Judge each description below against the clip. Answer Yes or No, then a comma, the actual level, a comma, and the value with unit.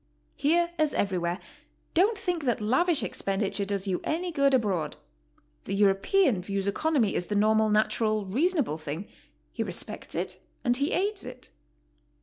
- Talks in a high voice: Yes, high, 220 Hz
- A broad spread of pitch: Yes, wide, 8.2 semitones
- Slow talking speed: No, average, 145 wpm